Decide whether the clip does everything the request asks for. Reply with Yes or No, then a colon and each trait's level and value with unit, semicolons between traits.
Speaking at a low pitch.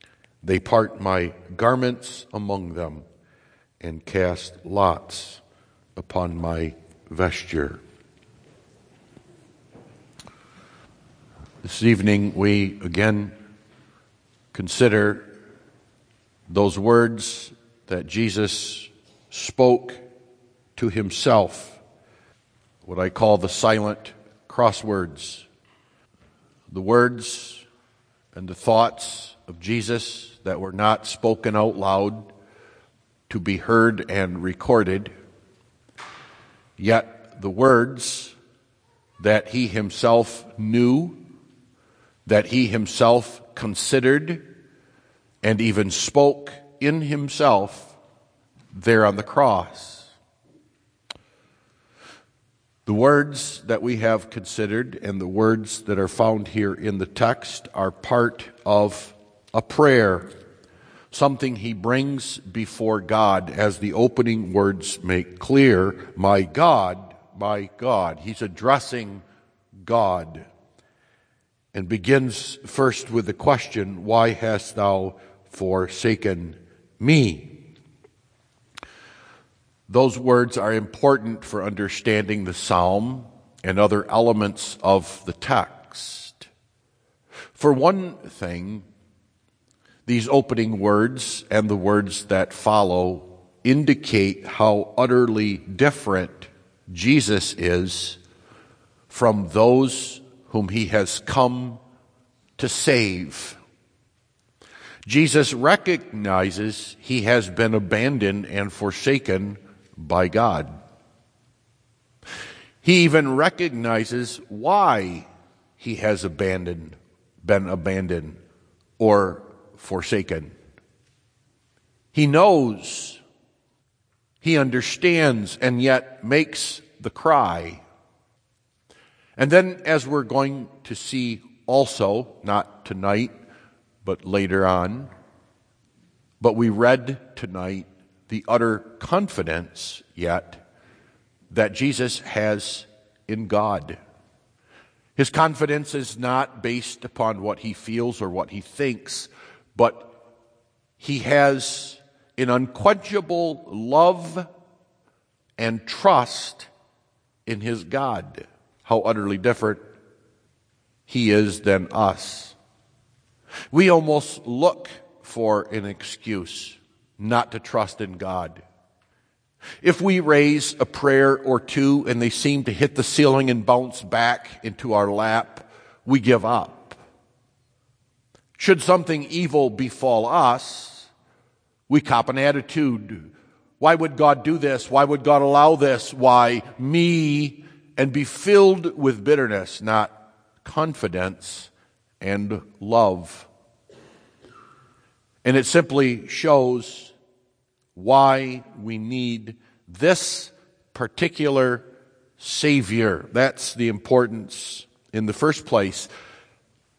Yes: low, 115 Hz